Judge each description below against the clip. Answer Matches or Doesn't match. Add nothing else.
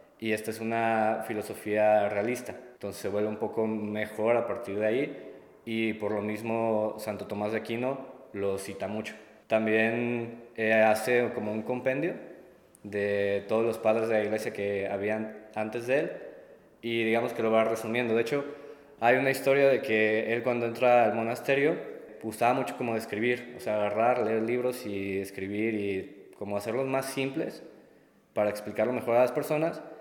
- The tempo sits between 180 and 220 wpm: Doesn't match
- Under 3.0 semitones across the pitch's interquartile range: Matches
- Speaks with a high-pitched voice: Doesn't match